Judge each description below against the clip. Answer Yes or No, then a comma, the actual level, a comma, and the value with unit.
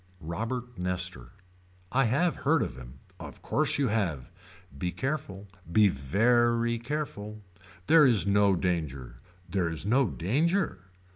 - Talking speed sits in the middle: No, slow, 130 wpm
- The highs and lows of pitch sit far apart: Yes, wide, 6.0 semitones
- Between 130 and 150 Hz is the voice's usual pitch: No, low, 105 Hz